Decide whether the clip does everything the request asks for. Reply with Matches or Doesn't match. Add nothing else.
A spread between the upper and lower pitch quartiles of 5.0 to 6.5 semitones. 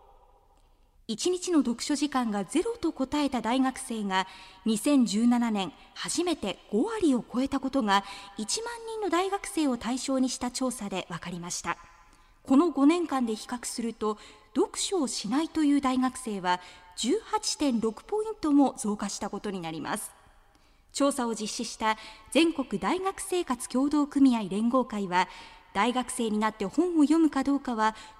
Matches